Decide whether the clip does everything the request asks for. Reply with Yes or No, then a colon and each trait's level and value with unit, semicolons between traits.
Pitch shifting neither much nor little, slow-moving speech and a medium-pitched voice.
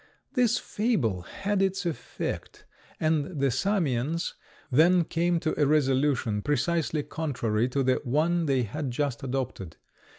Yes: average, 4.9 semitones; slow, 130 wpm; medium, 145 Hz